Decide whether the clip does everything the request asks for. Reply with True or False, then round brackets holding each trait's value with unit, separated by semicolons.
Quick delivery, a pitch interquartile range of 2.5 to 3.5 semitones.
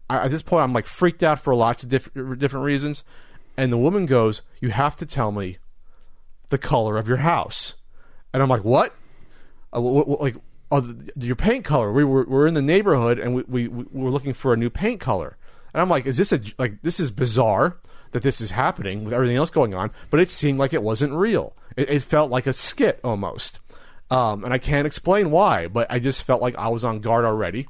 True (230 wpm; 3.2 semitones)